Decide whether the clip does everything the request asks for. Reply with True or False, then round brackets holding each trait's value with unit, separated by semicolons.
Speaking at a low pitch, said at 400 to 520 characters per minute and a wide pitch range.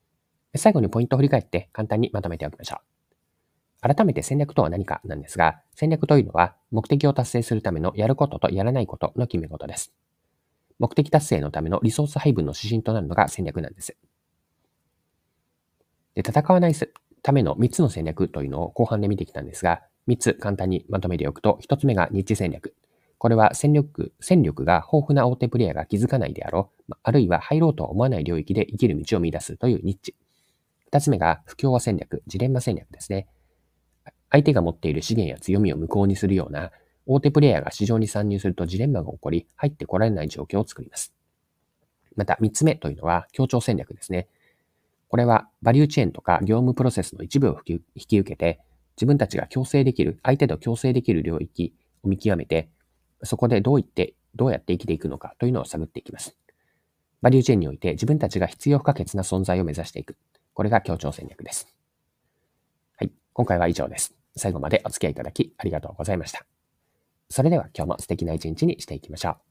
True (100 Hz; 415 characters per minute; 7.0 semitones)